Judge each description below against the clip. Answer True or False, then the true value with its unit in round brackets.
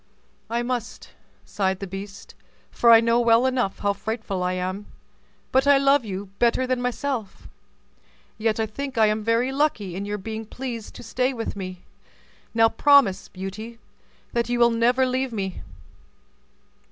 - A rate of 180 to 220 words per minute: False (160 wpm)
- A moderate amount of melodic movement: True (3.8 semitones)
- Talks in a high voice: True (230 Hz)